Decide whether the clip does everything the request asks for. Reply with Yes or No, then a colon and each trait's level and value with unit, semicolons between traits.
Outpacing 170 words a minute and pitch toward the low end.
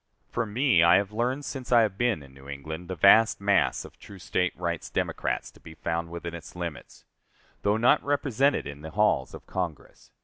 Yes: average, 200 wpm; very low, 95 Hz